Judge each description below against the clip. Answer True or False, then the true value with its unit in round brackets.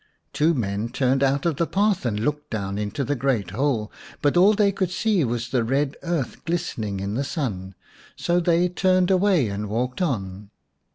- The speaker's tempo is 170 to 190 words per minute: True (185 wpm)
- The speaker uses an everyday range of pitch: False (8.1 semitones)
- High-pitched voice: False (135 Hz)